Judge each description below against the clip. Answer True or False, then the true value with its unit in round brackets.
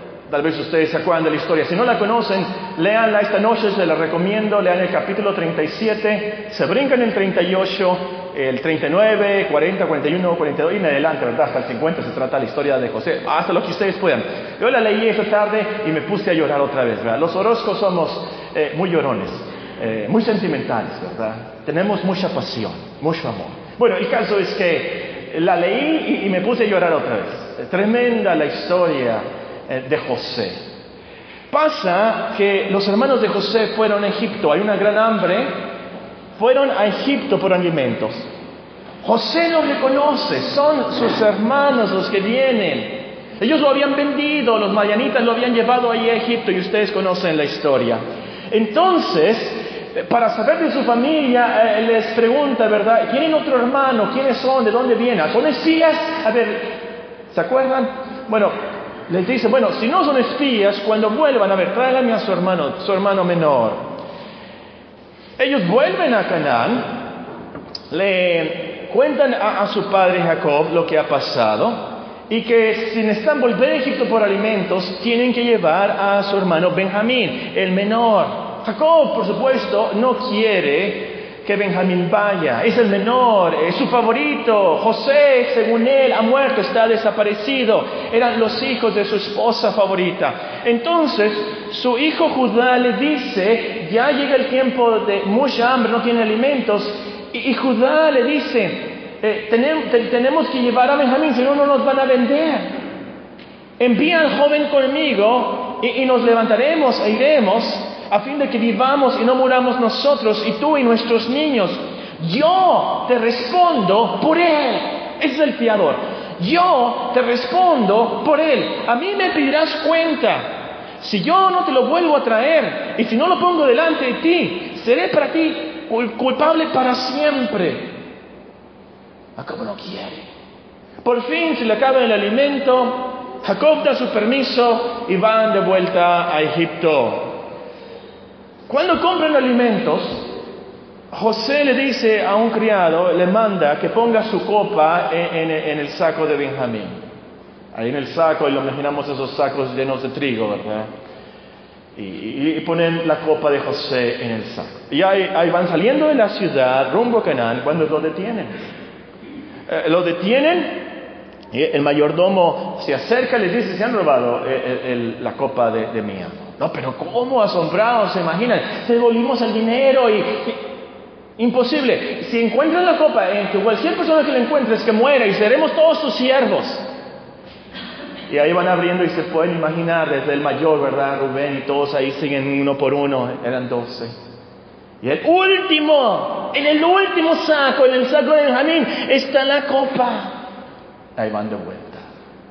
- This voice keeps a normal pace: True (160 wpm)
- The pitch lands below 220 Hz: False (230 Hz)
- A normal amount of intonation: False (6.1 semitones)